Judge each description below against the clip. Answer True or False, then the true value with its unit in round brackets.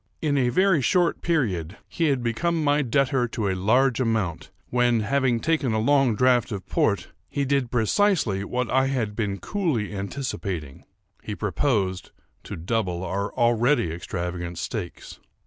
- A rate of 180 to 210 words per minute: False (145 wpm)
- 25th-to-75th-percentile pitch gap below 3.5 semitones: False (5.5 semitones)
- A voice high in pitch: False (120 Hz)